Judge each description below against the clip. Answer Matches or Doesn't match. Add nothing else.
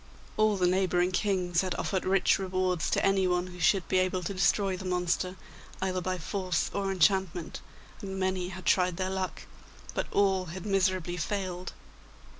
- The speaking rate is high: Doesn't match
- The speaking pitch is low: Doesn't match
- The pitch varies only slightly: Matches